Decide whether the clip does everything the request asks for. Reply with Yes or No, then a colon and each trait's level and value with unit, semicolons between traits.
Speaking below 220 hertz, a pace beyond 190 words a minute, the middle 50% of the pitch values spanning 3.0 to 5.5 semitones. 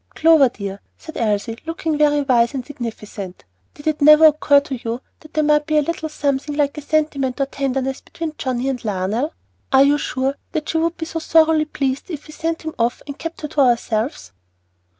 No: very high, 285 Hz; fast, 205 wpm; average, 3.5 semitones